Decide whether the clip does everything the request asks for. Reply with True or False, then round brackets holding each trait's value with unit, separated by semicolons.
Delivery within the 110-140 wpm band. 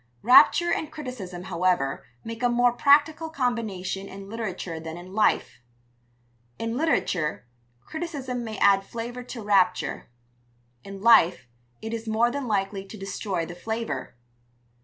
True (135 wpm)